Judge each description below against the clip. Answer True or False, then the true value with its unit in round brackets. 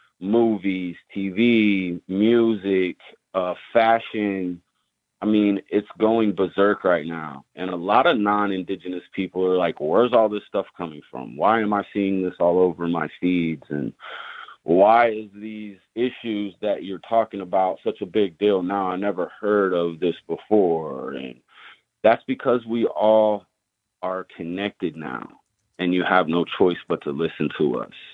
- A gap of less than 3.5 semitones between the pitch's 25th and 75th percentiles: True (2.9 semitones)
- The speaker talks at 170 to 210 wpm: False (155 wpm)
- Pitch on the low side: True (100 Hz)